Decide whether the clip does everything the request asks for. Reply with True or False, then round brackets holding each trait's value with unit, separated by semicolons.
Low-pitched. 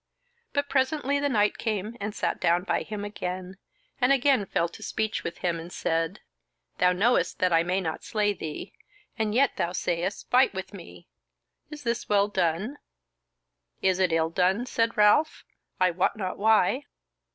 False (205 Hz)